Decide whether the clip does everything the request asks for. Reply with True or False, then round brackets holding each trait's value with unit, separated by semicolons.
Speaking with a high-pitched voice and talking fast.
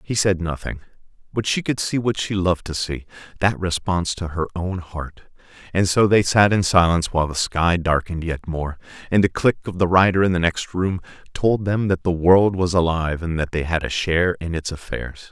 False (90 Hz; 220 wpm)